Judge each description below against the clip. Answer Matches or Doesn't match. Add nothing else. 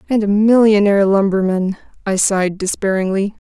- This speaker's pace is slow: Matches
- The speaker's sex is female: Matches